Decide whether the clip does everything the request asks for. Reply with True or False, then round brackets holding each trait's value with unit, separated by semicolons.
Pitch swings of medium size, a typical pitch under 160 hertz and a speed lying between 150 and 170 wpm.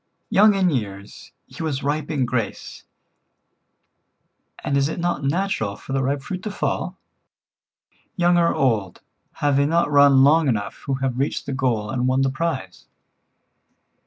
True (4.1 semitones; 140 Hz; 160 wpm)